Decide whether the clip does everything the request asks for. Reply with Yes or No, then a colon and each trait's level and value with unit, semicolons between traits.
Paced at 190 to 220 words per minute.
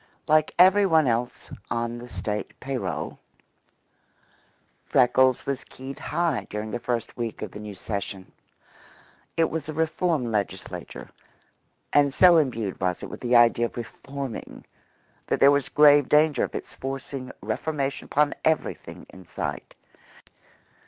No: average, 140 wpm